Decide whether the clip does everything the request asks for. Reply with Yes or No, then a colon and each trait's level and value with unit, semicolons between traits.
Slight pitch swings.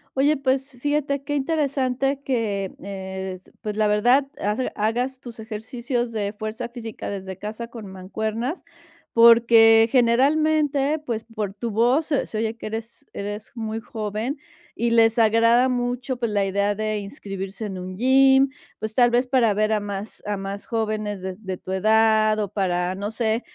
No: average, 3.3 semitones